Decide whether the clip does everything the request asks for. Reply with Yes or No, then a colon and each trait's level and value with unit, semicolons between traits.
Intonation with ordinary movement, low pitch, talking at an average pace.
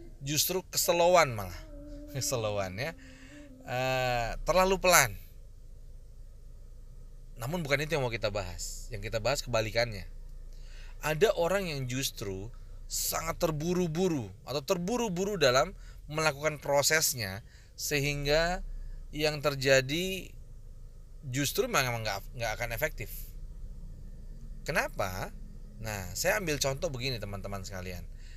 No: wide, 6.3 semitones; low, 125 Hz; average, 95 wpm